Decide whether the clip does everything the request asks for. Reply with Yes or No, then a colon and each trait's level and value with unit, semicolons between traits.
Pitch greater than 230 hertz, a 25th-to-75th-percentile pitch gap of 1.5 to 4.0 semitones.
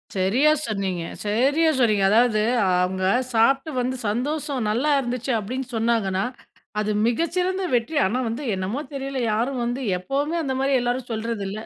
No: high, 240 Hz; average, 4.4 semitones